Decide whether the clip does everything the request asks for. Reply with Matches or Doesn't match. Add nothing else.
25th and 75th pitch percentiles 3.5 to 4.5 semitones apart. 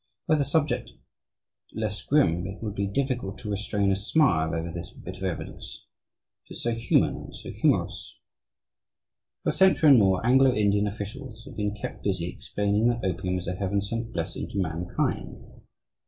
Matches